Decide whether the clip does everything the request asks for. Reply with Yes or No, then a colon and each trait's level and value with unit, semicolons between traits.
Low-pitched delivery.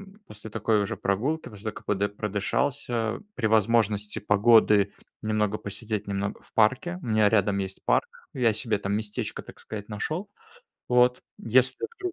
Yes: low, 110 Hz